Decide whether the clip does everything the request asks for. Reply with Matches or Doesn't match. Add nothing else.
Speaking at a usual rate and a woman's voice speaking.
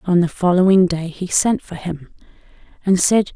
Matches